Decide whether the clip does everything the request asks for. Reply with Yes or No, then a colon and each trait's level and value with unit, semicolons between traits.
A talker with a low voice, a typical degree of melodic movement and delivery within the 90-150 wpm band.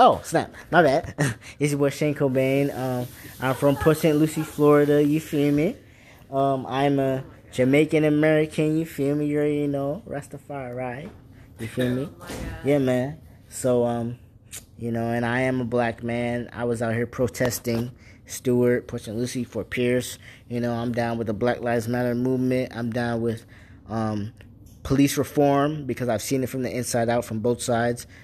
No: low, 125 Hz; average, 3.1 semitones; average, 185 wpm